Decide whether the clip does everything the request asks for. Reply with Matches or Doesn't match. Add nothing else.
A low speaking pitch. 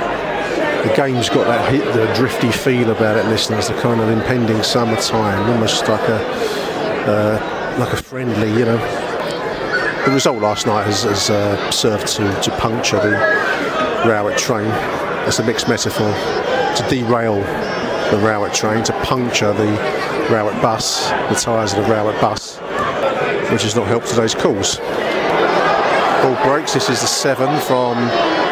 Matches